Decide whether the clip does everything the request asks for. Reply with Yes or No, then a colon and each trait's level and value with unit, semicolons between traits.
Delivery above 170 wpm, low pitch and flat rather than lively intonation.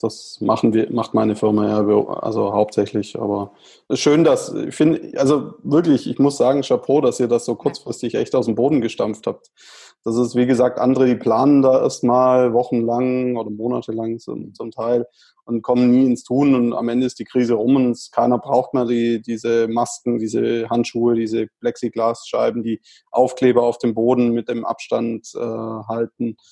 Yes: average, 180 wpm; low, 120 Hz; narrow, 1.5 semitones